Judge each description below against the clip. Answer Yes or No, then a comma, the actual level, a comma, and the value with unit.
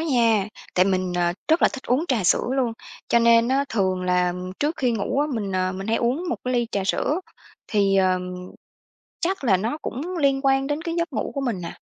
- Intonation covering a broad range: Yes, wide, 6.4 semitones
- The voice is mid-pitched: No, high, 235 Hz